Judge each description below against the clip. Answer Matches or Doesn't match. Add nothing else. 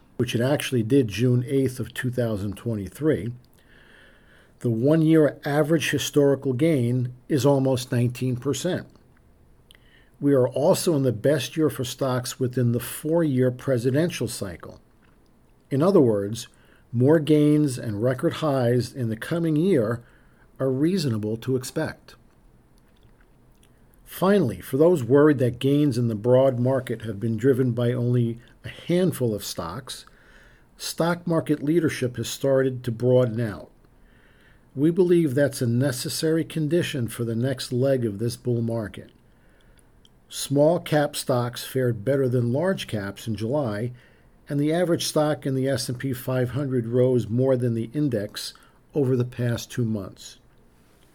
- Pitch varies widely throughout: Doesn't match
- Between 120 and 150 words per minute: Matches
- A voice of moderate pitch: Doesn't match